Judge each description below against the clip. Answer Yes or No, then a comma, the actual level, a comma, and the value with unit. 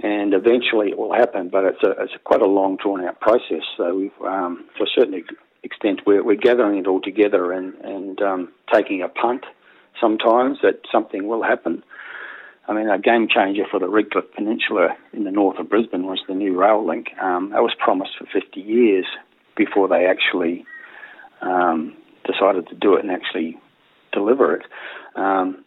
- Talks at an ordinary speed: Yes, average, 185 wpm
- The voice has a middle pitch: No, low, 120 Hz